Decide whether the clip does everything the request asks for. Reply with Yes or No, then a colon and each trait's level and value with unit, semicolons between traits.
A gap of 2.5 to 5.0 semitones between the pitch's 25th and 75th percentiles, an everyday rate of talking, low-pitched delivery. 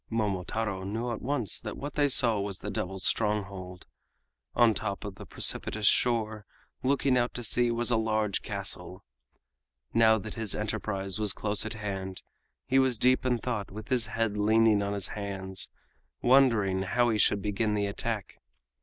Yes: average, 2.8 semitones; average, 170 wpm; low, 110 Hz